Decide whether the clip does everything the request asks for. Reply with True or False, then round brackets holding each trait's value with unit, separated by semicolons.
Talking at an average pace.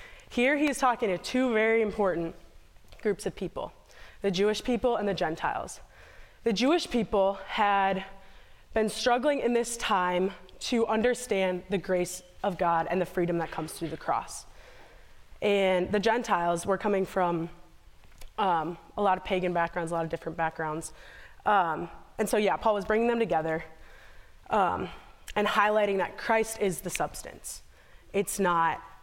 True (155 wpm)